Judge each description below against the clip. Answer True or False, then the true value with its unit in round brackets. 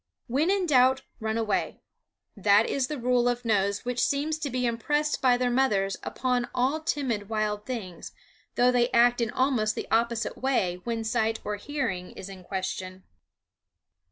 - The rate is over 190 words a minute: False (165 wpm)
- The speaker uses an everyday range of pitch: True (3.7 semitones)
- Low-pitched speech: False (240 Hz)